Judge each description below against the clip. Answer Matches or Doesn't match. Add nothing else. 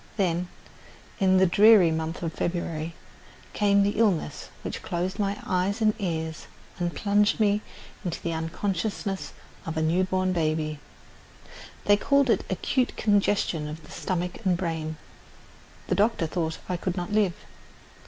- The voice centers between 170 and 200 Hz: Matches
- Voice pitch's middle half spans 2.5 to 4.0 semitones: Matches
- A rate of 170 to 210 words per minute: Doesn't match